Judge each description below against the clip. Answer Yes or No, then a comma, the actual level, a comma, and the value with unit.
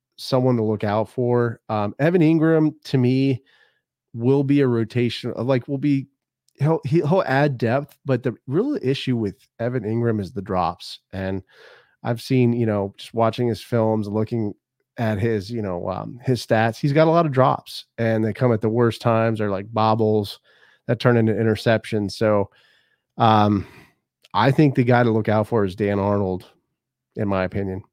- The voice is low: Yes, low, 115 Hz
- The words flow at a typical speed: Yes, average, 180 wpm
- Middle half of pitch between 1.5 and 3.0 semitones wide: No, average, 3.5 semitones